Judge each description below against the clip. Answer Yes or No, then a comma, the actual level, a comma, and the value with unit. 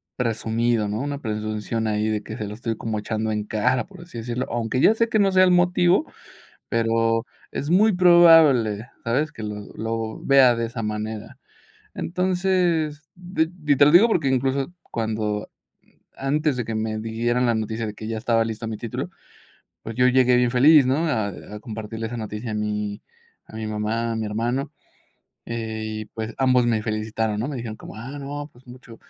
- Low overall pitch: Yes, low, 115 Hz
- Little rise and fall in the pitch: No, average, 4.5 semitones